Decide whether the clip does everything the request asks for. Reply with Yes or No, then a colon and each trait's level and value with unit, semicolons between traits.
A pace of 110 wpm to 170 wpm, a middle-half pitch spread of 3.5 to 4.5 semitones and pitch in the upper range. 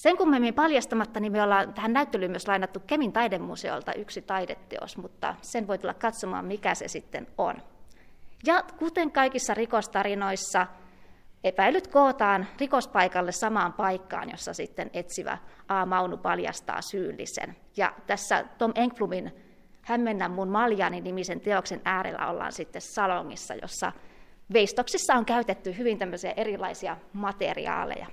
Yes: average, 130 wpm; average, 4.1 semitones; high, 205 Hz